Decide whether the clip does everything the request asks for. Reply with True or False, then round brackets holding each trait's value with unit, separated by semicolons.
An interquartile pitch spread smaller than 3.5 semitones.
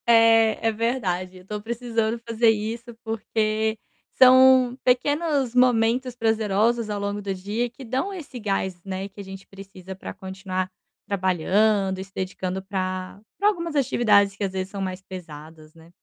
False (3.8 semitones)